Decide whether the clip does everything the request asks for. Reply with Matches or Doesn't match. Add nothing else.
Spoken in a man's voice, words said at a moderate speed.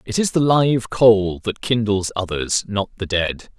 Matches